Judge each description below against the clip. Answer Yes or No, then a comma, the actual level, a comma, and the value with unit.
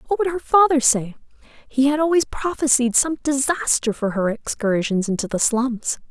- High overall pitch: Yes, very high, 265 Hz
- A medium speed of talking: Yes, average, 165 wpm